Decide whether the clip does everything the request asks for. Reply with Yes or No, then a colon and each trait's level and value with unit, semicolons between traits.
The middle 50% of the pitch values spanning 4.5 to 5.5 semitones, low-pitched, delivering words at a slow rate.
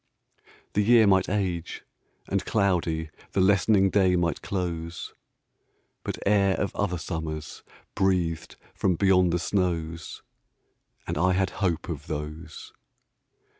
No: average, 2.9 semitones; very low, 90 Hz; slow, 120 wpm